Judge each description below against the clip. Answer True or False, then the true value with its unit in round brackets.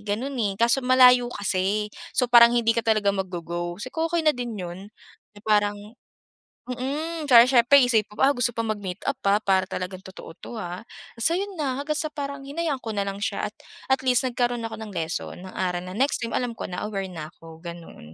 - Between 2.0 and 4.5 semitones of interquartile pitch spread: False (5.3 semitones)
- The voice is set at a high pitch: True (230 Hz)